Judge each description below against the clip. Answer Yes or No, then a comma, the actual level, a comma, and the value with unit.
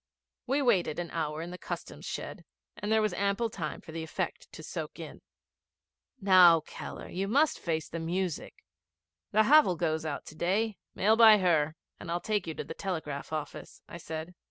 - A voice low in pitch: No, medium, 175 Hz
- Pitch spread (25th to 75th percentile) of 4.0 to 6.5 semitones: Yes, average, 4.3 semitones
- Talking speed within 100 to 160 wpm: No, average, 180 wpm